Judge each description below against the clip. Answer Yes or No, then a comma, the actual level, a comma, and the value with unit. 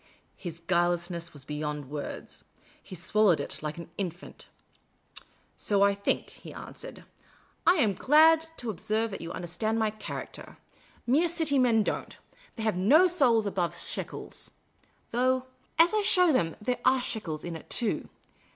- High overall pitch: Yes, high, 210 Hz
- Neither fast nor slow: Yes, average, 160 wpm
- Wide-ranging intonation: Yes, wide, 7.0 semitones